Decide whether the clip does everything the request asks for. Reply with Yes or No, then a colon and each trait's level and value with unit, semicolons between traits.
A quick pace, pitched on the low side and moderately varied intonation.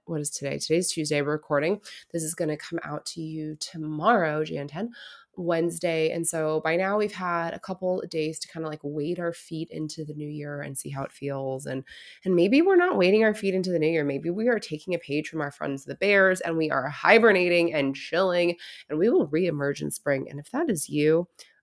No: fast, 235 wpm; medium, 160 Hz; average, 3.1 semitones